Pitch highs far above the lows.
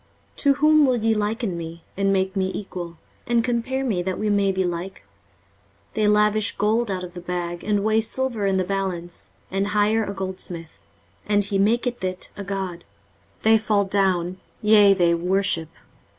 No: average, 2.8 semitones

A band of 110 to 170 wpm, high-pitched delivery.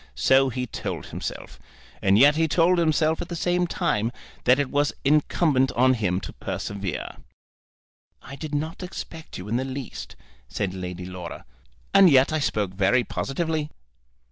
No: average, 160 wpm; low, 135 Hz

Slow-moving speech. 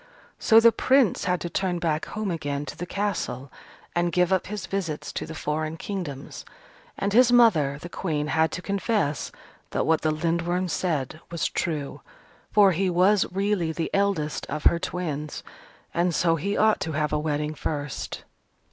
No: average, 175 wpm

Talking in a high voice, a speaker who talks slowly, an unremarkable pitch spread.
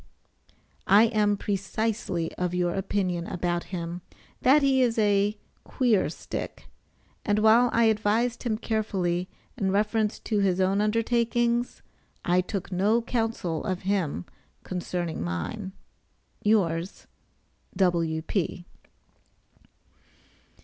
Yes: high, 200 Hz; slow, 105 wpm; average, 3.8 semitones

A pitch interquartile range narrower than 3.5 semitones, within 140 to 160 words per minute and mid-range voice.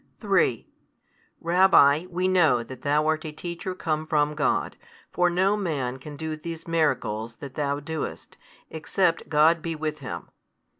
Yes: average, 2.8 semitones; average, 155 wpm; medium, 155 Hz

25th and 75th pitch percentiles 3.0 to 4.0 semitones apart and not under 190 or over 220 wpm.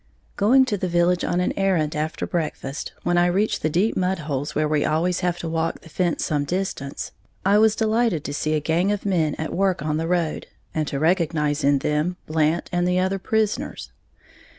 Yes: average, 3.5 semitones; fast, 205 wpm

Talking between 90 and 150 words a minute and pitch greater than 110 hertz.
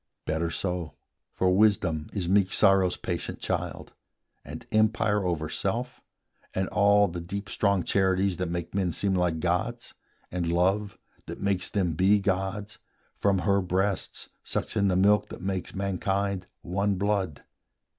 No: average, 145 wpm; very low, 95 Hz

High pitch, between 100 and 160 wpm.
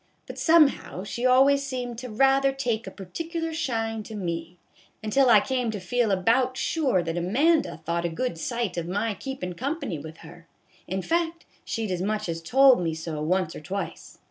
No: high, 225 Hz; average, 190 wpm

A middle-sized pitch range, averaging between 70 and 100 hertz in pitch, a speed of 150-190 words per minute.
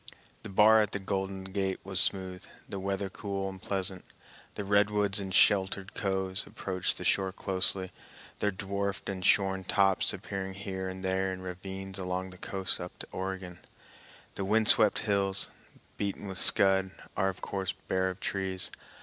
No: narrow, 0.9 semitones; very low, 95 Hz; average, 165 wpm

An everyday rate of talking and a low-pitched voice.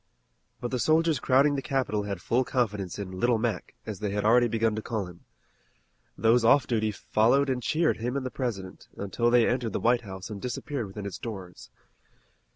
Yes: average, 195 wpm; low, 115 Hz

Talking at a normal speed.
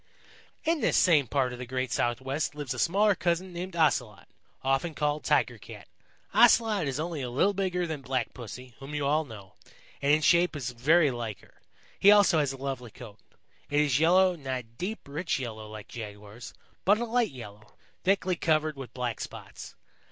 Yes: average, 190 wpm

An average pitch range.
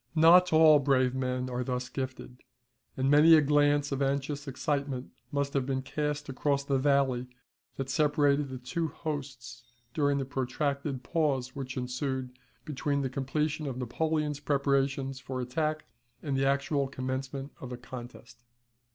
No: narrow, 2.1 semitones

